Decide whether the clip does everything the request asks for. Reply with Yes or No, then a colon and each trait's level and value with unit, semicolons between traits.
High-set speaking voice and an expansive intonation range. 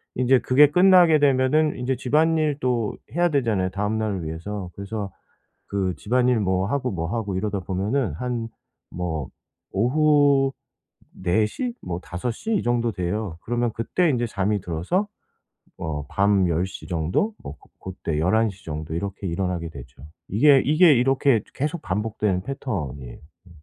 No: low, 105 Hz; wide, 6.6 semitones